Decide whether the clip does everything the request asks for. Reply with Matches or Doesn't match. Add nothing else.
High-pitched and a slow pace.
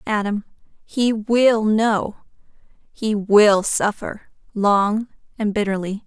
Matches